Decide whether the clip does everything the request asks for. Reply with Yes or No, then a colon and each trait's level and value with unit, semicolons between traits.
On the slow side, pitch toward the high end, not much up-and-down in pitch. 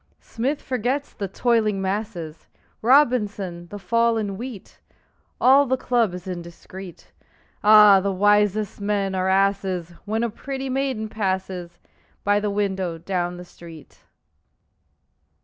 No: slow, 125 wpm; high, 205 Hz; average, 3.5 semitones